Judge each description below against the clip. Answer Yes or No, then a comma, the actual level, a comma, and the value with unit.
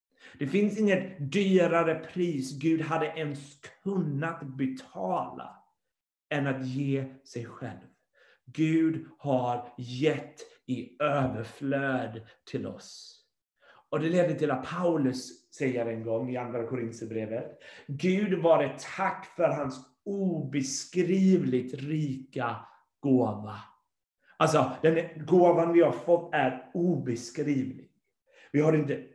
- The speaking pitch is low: No, medium, 145 Hz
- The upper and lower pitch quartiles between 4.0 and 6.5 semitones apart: Yes, average, 4.6 semitones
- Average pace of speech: No, slow, 110 wpm